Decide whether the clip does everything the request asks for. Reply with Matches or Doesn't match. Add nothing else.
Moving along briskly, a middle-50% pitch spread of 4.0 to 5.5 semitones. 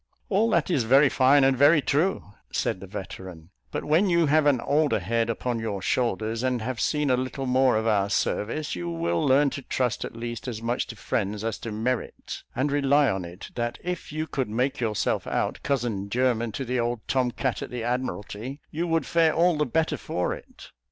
Matches